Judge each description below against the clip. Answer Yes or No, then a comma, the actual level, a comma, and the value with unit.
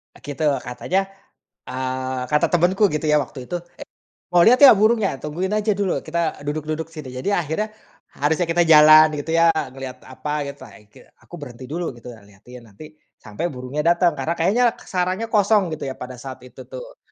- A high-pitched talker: No, medium, 155 Hz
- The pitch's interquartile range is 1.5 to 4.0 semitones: No, wide, 5.6 semitones